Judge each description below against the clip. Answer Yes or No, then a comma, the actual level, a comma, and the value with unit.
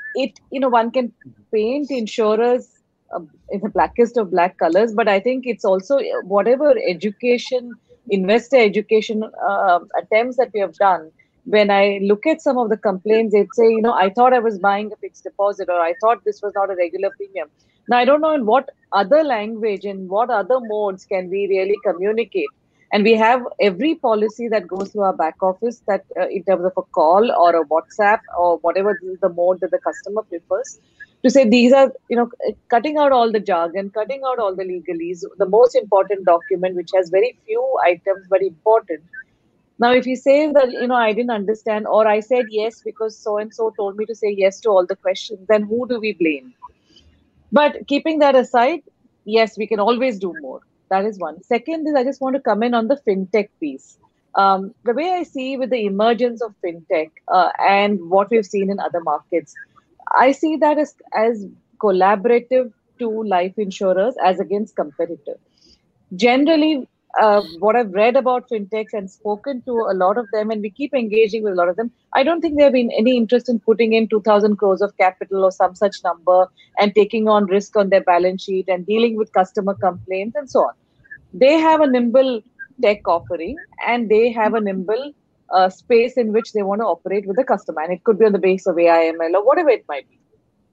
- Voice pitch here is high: Yes, high, 215 Hz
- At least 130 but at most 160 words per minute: No, fast, 205 wpm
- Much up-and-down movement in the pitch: No, average, 4.1 semitones